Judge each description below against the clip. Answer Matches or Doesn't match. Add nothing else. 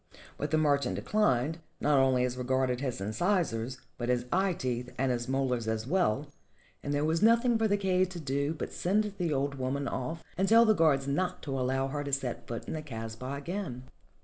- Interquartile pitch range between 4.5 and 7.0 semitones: Matches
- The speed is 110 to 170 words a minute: Doesn't match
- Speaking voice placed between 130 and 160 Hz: Matches